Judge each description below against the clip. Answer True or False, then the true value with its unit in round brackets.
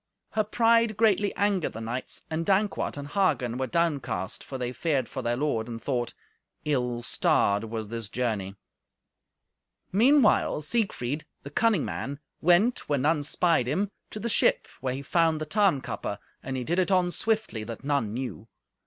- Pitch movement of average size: False (7.9 semitones)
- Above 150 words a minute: True (165 wpm)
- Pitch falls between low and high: True (145 Hz)